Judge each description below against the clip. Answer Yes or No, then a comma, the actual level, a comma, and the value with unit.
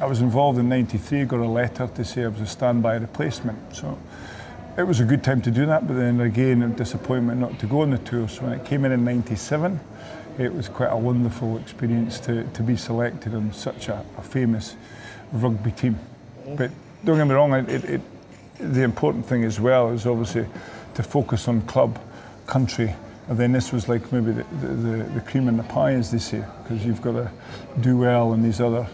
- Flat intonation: Yes, narrow, 1.8 semitones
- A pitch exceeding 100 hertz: Yes, low, 120 Hz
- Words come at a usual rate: No, fast, 215 wpm